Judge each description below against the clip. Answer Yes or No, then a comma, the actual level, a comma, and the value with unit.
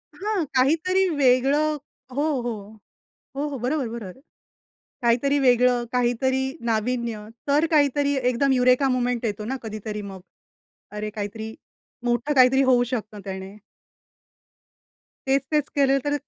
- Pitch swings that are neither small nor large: Yes, average, 3.4 semitones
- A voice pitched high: Yes, very high, 250 Hz